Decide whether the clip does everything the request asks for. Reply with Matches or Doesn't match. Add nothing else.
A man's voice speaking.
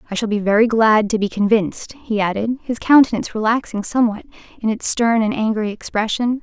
Doesn't match